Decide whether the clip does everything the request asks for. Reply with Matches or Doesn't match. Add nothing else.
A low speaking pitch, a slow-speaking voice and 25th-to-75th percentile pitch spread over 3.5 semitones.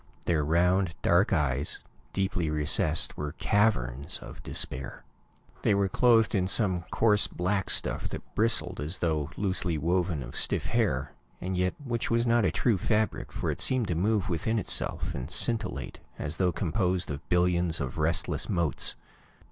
Doesn't match